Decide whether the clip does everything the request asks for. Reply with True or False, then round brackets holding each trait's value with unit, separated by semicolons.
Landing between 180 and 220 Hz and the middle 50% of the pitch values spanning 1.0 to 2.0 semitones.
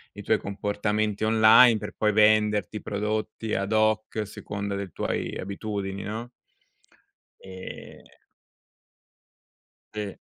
False (105 Hz; 1.4 semitones)